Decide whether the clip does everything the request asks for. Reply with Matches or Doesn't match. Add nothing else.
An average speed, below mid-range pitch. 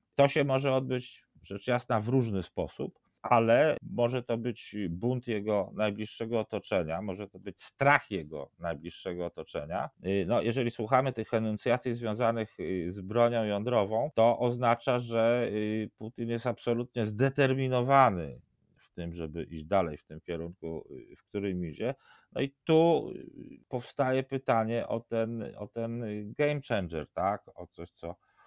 Matches